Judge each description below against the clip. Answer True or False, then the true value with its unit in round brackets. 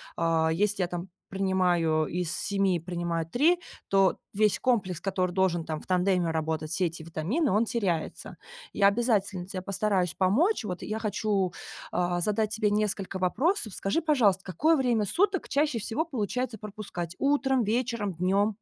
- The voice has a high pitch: True (195 Hz)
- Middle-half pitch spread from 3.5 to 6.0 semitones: True (4.0 semitones)